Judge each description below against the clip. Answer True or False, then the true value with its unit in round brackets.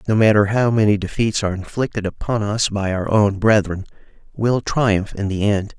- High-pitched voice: False (105 Hz)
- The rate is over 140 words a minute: True (185 wpm)